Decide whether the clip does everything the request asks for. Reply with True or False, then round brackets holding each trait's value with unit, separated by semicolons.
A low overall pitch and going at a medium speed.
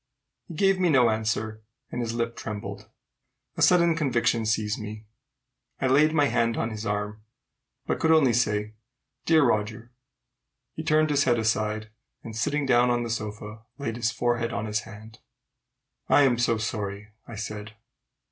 True (115 Hz; 160 wpm)